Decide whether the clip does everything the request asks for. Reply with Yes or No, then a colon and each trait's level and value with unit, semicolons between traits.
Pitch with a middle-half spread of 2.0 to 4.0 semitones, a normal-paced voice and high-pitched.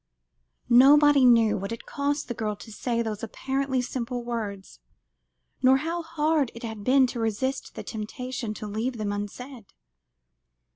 Yes: average, 3.5 semitones; average, 150 wpm; high, 240 Hz